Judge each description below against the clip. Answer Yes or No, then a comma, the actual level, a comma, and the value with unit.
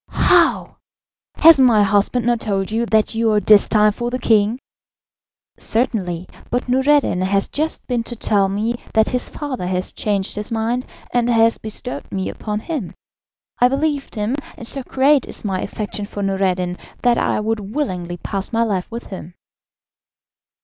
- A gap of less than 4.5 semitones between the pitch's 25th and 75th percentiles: Yes, average, 3.7 semitones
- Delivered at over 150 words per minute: Yes, average, 165 wpm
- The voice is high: Yes, high, 220 Hz